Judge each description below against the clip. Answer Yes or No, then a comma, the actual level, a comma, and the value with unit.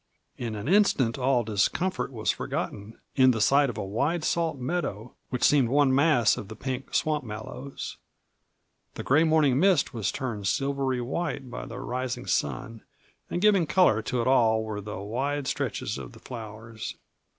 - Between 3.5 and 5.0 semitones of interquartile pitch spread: Yes, average, 4.6 semitones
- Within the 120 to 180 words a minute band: Yes, average, 170 wpm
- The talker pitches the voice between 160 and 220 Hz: No, low, 125 Hz